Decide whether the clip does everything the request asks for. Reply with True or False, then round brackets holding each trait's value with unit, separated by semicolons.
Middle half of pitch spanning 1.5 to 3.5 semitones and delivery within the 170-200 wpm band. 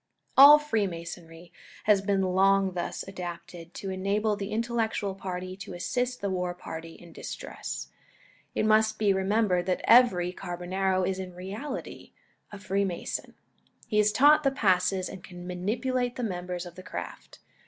False (3.2 semitones; 150 wpm)